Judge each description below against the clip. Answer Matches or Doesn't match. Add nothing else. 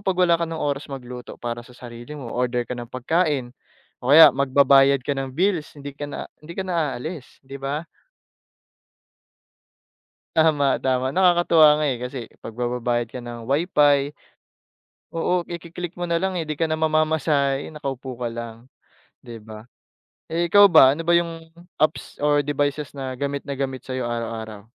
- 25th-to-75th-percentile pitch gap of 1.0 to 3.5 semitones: Doesn't match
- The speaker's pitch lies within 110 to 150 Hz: Matches